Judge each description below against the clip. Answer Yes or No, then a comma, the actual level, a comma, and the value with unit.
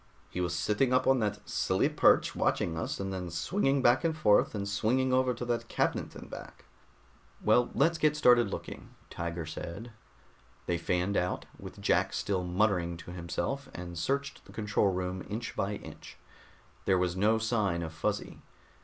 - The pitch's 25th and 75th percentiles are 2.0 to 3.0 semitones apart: No, wide, 5.5 semitones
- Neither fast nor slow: Yes, average, 170 wpm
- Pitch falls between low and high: No, low, 105 Hz